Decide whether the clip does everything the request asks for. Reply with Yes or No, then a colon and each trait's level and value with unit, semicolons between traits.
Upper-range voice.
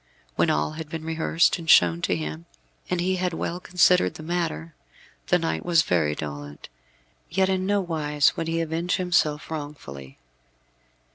No: medium, 160 Hz